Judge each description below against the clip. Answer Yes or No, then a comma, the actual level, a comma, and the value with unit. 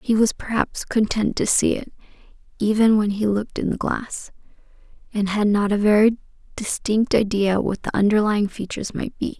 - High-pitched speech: Yes, high, 210 Hz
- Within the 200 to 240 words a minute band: No, average, 170 wpm